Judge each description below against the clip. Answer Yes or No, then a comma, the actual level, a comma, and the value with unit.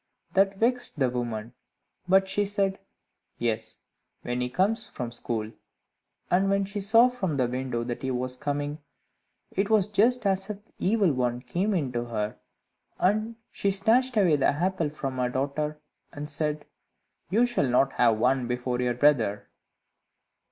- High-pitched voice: No, medium, 150 Hz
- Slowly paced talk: No, average, 160 wpm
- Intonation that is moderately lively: No, wide, 8.0 semitones